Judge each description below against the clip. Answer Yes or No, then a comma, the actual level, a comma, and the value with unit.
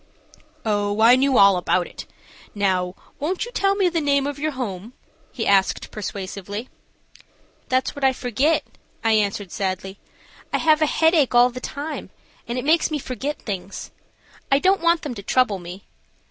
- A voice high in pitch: Yes, very high, 250 Hz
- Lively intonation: Yes, wide, 6.7 semitones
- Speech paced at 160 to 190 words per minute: Yes, average, 170 wpm